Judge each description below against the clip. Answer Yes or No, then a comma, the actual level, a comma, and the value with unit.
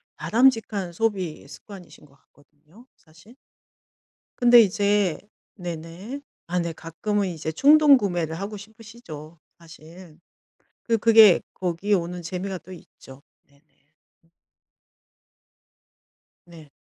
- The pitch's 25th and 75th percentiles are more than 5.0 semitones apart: No, average, 4.6 semitones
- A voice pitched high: No, medium, 180 Hz